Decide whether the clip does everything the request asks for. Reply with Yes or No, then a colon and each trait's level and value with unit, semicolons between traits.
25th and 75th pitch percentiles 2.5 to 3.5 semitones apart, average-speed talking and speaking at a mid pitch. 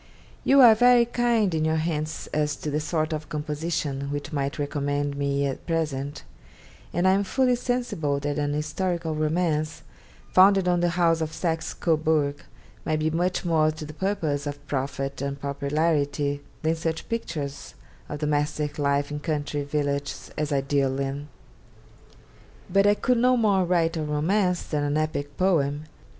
Yes: average, 3.2 semitones; average, 165 wpm; medium, 155 Hz